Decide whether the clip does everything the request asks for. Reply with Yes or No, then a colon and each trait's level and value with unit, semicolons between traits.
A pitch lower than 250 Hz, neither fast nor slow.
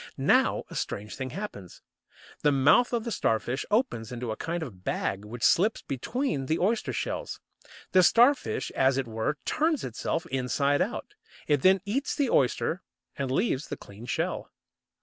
Yes: medium, 140 Hz; average, 165 wpm